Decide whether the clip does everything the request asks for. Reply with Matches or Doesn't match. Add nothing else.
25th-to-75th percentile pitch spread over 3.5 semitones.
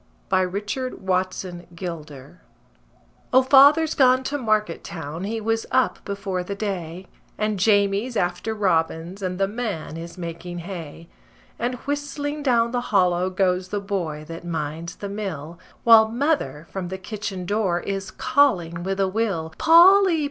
Matches